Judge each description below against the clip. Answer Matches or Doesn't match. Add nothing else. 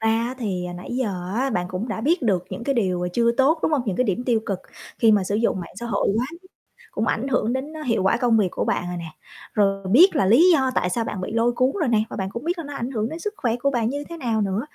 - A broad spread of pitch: Doesn't match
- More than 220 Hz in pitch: Matches